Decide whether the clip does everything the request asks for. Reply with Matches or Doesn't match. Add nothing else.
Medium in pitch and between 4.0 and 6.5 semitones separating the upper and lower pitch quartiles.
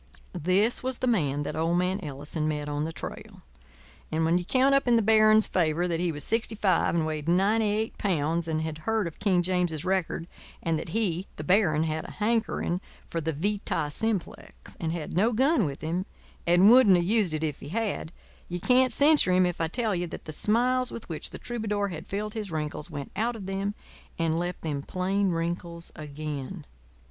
Matches